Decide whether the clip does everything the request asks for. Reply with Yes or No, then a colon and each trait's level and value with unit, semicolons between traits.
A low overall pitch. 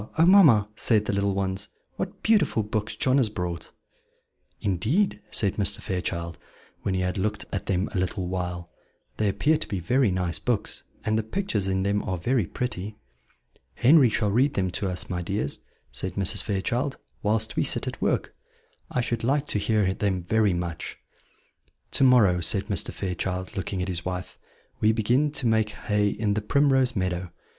Yes: low, 100 Hz